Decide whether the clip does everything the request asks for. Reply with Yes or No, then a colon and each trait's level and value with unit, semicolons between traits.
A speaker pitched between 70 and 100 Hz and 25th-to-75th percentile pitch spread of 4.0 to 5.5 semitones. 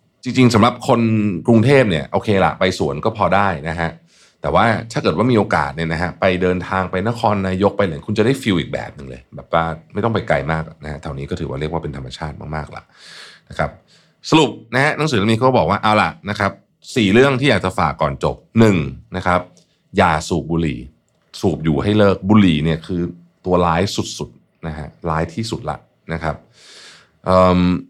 Yes: very low, 90 Hz; average, 4.6 semitones